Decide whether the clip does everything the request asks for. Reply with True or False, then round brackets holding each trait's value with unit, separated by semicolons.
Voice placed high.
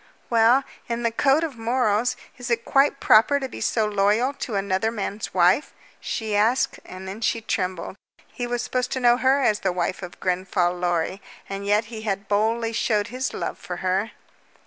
True (220 Hz)